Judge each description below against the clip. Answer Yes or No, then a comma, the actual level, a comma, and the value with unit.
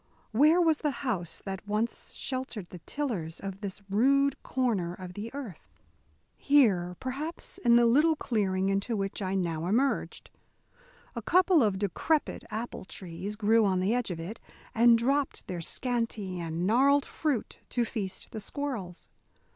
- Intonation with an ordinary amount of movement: No, wide, 5.8 semitones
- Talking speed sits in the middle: Yes, average, 155 wpm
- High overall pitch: Yes, high, 220 Hz